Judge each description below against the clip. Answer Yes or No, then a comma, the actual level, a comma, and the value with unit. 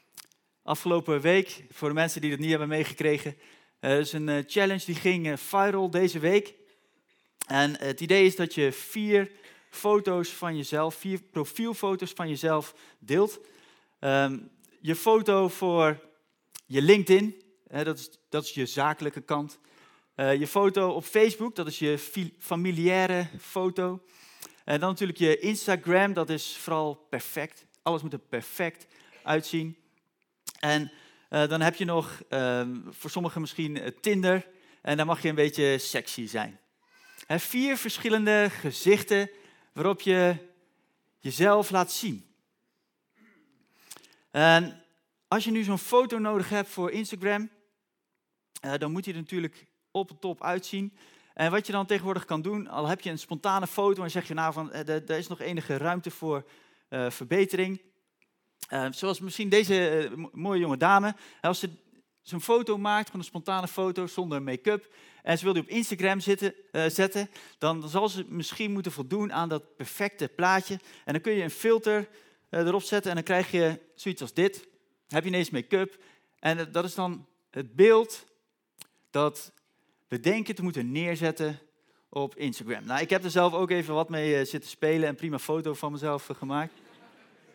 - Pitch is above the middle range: No, medium, 175 Hz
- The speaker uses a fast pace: No, average, 160 wpm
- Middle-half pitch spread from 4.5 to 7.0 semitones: No, average, 4.1 semitones